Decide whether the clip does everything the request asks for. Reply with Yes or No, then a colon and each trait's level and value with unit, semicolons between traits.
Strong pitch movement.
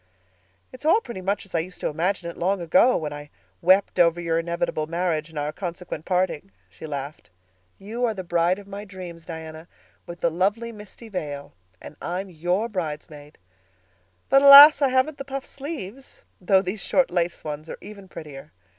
No: average, 4.3 semitones